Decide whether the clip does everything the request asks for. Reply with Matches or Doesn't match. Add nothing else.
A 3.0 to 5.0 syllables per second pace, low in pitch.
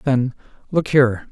Matches